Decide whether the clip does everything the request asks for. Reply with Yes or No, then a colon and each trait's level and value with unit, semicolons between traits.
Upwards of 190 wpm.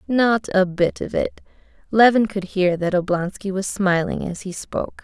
No: average, 180 wpm